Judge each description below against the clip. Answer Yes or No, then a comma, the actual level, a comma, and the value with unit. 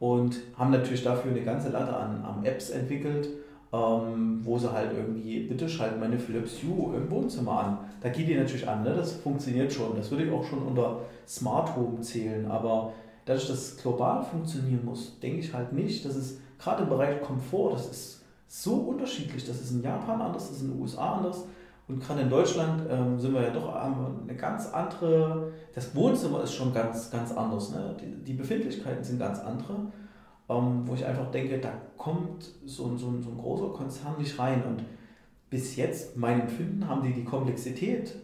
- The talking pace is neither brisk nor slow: No, fast, 195 wpm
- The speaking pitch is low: Yes, low, 130 Hz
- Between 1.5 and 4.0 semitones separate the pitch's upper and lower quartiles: Yes, average, 3.6 semitones